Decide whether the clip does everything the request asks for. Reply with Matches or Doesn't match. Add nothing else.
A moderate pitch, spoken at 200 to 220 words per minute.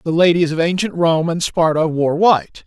Matches